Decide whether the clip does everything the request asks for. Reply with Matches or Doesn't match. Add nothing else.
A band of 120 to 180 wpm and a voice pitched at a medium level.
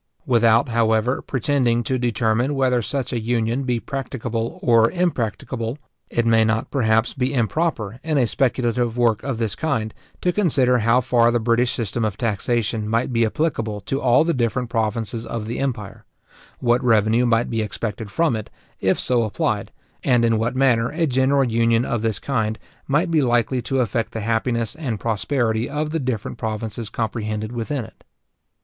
Doesn't match